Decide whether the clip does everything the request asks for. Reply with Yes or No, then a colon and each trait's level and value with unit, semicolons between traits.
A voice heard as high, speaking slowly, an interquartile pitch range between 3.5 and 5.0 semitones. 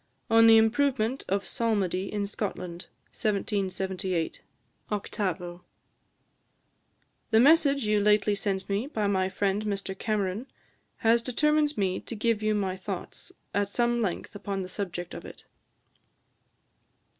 No: high, 205 Hz; slow, 125 wpm; average, 2.9 semitones